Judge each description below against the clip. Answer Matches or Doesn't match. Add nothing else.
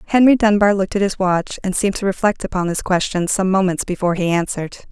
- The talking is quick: Matches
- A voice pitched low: Doesn't match